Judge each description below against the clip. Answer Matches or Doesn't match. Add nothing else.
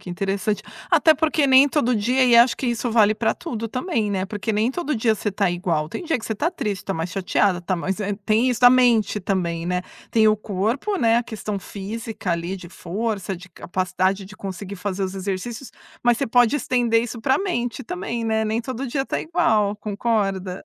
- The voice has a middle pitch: Doesn't match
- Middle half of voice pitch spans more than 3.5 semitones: Matches